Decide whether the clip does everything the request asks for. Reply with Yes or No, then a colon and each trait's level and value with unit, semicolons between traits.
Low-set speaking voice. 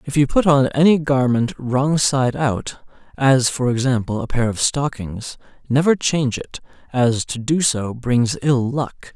Yes: low, 130 Hz